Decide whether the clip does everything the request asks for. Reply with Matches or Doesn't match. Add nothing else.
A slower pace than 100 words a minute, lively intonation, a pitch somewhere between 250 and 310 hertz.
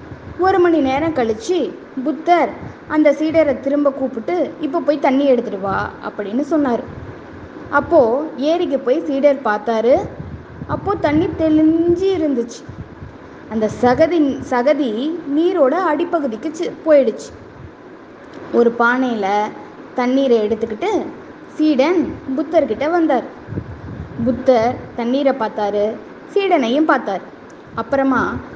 Doesn't match